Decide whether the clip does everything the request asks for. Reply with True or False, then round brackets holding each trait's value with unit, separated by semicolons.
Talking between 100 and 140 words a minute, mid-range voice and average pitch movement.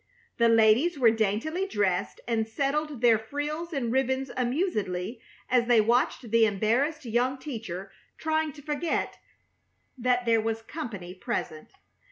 False (135 wpm; 240 Hz; 4.7 semitones)